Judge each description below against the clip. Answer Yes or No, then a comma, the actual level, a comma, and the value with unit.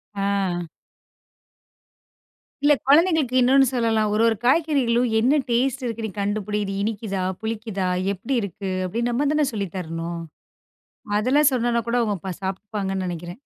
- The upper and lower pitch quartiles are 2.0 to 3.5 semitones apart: No, average, 4.4 semitones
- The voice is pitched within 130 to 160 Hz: No, high, 220 Hz